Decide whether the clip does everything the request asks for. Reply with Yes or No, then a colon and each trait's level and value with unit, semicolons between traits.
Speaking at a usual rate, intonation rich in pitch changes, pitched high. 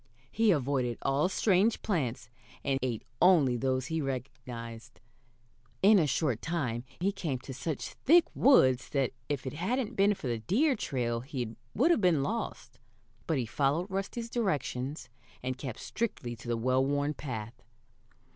No: average, 155 wpm; wide, 7.1 semitones; medium, 140 Hz